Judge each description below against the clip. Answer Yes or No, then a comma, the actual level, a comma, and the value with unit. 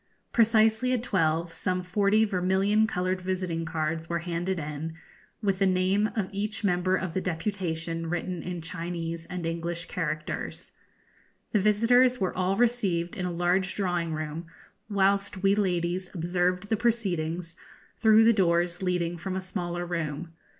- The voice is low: No, medium, 180 Hz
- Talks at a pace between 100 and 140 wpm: No, average, 150 wpm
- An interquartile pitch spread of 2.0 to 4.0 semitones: Yes, average, 2.8 semitones